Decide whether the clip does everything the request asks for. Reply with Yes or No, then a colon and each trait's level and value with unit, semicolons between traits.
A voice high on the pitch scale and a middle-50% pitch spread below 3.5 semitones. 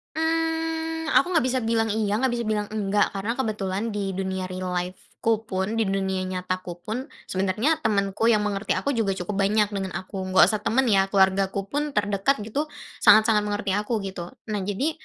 Yes: high, 205 Hz; average, 3.1 semitones